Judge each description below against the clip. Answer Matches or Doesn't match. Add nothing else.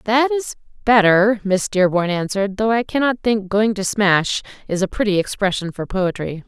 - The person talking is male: Doesn't match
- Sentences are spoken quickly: Doesn't match